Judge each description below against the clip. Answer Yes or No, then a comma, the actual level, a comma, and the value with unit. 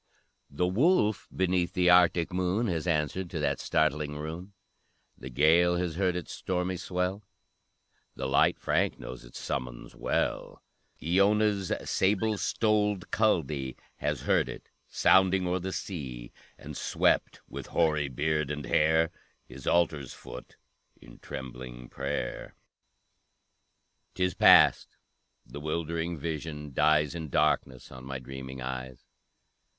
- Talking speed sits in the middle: No, slow, 125 wpm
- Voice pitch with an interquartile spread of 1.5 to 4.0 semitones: No, average, 5.0 semitones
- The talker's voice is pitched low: Yes, very low, 80 Hz